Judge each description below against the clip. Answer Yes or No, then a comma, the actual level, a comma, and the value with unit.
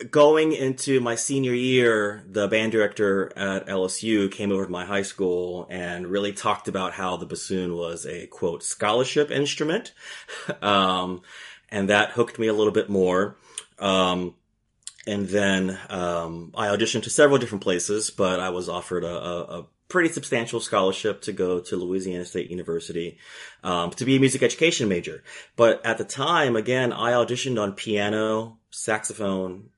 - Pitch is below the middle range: Yes, low, 100 Hz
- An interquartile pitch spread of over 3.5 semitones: Yes, average, 4.2 semitones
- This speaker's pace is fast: No, average, 160 wpm